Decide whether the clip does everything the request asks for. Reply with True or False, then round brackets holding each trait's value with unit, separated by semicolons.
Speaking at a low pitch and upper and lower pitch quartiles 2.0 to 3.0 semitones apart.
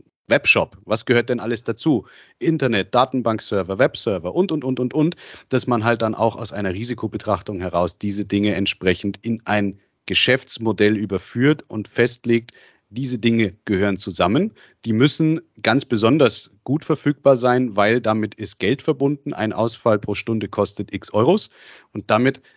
False (115 Hz; 3.8 semitones)